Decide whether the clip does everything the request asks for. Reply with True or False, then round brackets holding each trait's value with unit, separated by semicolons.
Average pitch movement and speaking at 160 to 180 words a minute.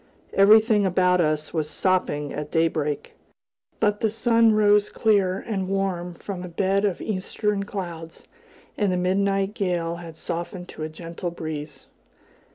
False (3.4 semitones; 145 wpm)